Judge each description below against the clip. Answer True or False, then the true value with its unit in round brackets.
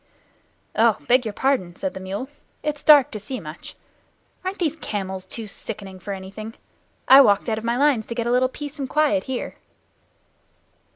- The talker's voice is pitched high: True (235 Hz)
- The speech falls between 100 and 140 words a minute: False (185 wpm)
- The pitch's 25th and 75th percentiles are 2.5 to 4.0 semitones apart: False (5.3 semitones)